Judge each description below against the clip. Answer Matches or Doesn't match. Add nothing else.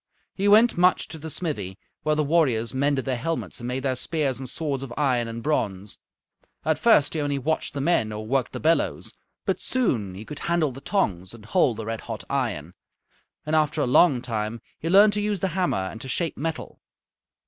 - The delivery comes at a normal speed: Doesn't match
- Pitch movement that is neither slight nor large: Doesn't match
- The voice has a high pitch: Doesn't match